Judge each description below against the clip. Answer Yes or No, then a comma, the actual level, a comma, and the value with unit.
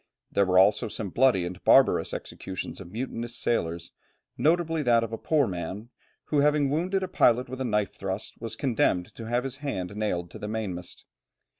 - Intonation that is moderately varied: No, wide, 5.9 semitones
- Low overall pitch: Yes, low, 115 Hz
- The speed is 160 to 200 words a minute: Yes, average, 185 wpm